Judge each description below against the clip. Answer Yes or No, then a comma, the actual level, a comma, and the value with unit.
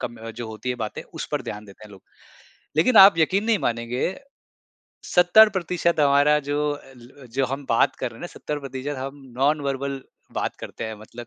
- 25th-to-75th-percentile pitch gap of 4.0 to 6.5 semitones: Yes, average, 4.4 semitones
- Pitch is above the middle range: No, low, 135 Hz